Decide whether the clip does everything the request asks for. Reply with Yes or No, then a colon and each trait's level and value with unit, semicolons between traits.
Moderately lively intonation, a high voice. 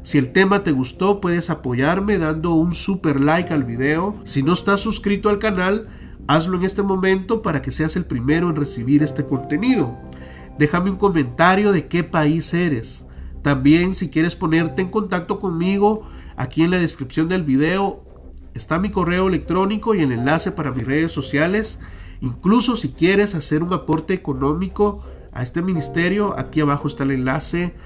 No: average, 4.9 semitones; medium, 165 Hz